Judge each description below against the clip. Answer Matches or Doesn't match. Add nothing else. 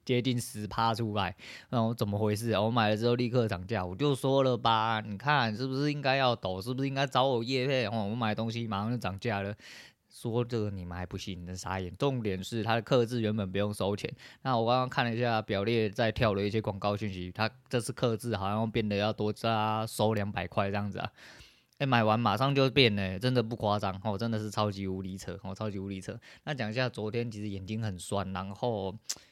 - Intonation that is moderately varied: Matches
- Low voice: Matches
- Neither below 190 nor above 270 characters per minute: Doesn't match